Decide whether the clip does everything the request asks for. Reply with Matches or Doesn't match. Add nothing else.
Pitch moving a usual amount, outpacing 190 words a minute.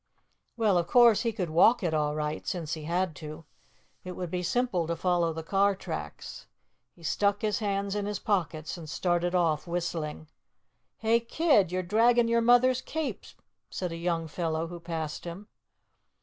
Doesn't match